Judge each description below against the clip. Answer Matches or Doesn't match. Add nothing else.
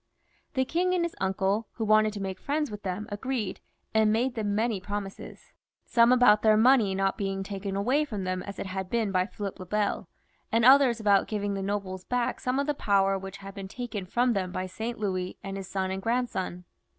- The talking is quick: Matches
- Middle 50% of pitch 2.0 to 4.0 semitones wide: Matches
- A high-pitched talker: Matches